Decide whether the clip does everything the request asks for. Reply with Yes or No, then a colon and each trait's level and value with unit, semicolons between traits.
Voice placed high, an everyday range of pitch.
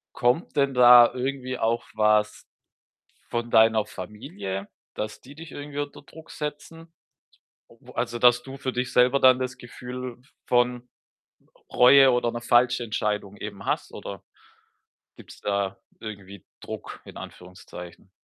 No: low, 120 Hz; average, 3.3 semitones